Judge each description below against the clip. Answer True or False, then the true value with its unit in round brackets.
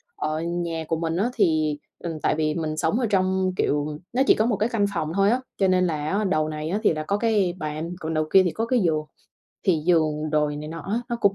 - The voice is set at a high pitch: False (170 Hz)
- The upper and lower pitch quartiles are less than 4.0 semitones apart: False (4.3 semitones)